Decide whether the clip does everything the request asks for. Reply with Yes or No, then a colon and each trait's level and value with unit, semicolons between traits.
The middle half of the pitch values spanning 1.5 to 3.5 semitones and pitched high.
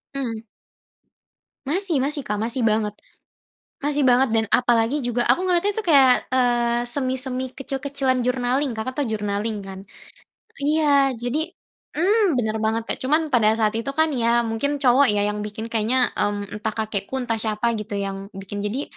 No: average, 4.0 semitones; high, 245 Hz